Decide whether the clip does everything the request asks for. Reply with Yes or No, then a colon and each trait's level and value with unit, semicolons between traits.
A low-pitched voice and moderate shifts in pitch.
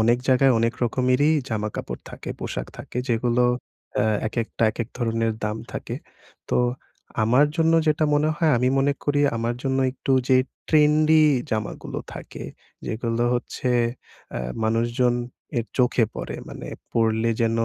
Yes: low, 120 Hz; average, 3.0 semitones